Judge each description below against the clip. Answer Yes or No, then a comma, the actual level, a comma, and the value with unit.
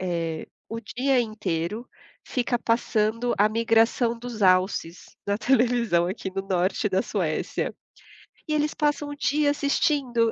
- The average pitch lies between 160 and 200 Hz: No, high, 230 Hz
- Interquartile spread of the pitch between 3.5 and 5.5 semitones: Yes, average, 4.6 semitones